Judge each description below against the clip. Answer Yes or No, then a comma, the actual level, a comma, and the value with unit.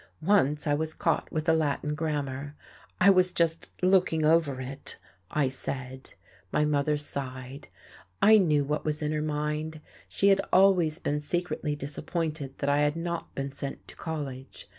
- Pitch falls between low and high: Yes, medium, 150 Hz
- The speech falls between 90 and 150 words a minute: No, average, 160 wpm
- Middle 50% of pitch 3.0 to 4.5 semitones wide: No, narrow, 2.5 semitones